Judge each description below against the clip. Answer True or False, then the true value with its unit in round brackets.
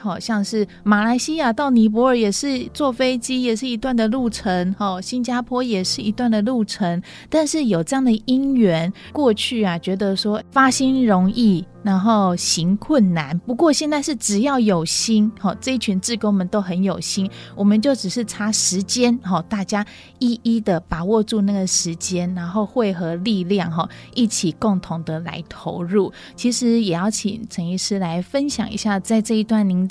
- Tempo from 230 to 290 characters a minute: True (255 characters per minute)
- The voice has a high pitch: True (215 Hz)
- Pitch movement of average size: True (4.3 semitones)